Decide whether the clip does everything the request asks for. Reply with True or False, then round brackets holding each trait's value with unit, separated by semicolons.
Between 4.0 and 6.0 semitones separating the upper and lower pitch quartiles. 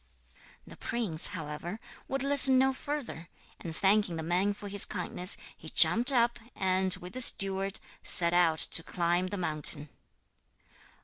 True (5.1 semitones)